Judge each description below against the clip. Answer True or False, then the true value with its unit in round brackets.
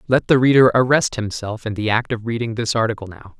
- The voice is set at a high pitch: False (115 Hz)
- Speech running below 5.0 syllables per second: False (5.9 syllables/s)